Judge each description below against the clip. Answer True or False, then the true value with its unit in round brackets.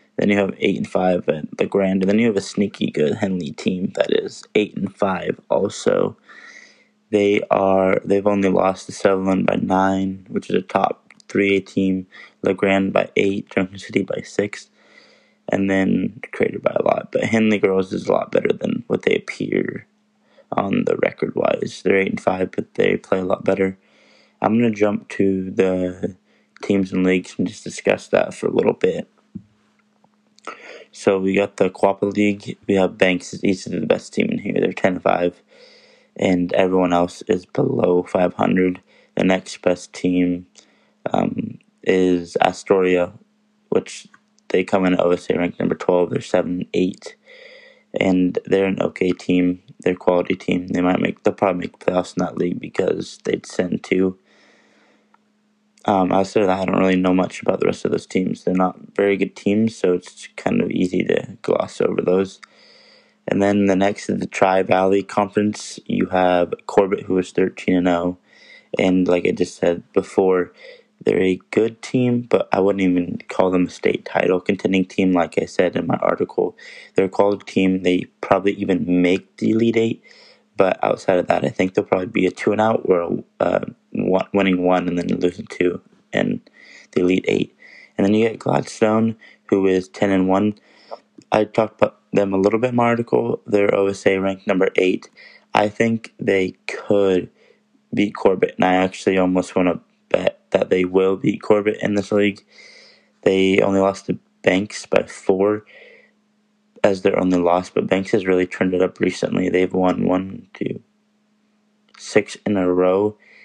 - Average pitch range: False (2.3 semitones)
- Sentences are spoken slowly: False (180 wpm)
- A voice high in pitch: False (95 Hz)